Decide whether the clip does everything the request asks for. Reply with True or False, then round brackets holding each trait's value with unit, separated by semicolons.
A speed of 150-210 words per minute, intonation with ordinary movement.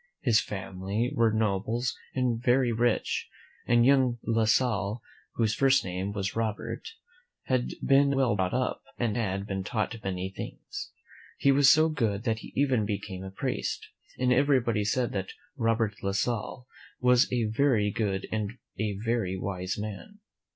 True (160 wpm; 3.9 semitones)